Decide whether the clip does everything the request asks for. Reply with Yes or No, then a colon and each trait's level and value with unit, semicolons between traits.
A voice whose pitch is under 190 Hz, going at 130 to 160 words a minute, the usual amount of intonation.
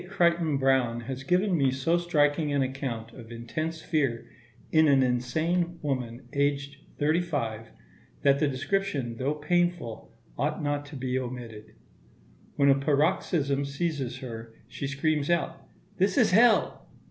Yes: medium, 140 Hz; average, 140 wpm; average, 4.1 semitones